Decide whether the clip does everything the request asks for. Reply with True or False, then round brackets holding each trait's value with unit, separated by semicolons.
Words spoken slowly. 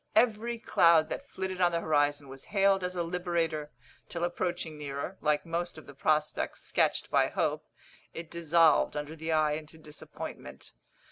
False (160 wpm)